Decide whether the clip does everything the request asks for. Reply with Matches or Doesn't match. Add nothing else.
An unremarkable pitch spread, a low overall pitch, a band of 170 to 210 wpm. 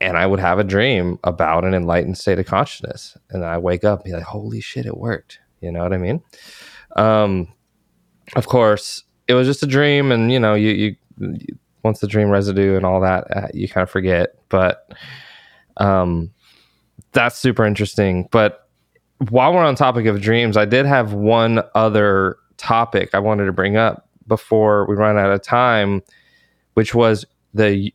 Matches